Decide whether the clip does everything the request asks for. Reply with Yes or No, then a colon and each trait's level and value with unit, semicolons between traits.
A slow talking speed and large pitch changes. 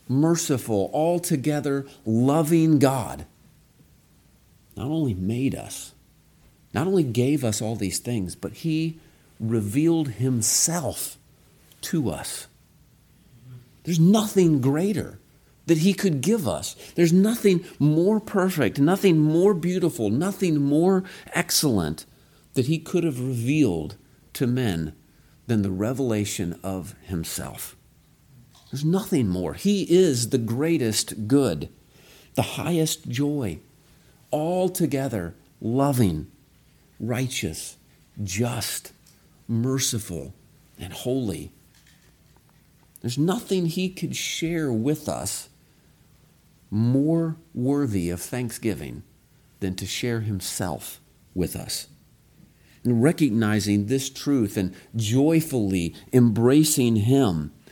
Yes: slow, 100 wpm; wide, 6.3 semitones